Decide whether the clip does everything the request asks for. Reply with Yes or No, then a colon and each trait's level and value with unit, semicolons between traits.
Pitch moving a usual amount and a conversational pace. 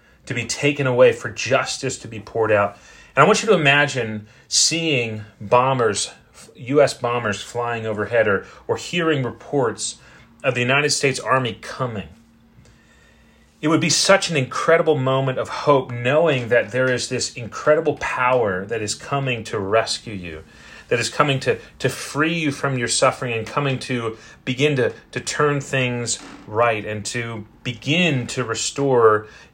Yes: average, 4.0 semitones; average, 160 wpm